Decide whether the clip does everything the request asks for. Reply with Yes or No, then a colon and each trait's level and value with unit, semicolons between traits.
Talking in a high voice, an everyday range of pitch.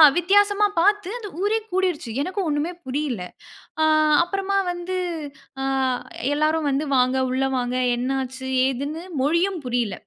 No: very high, 310 Hz; wide, 6.3 semitones